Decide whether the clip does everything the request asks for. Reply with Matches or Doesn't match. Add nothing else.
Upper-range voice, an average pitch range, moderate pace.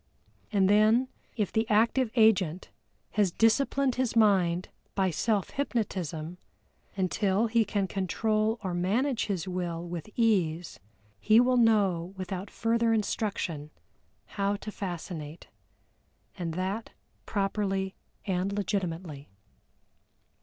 Doesn't match